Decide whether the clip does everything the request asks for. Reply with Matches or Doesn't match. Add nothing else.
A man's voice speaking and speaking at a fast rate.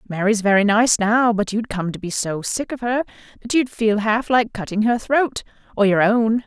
Doesn't match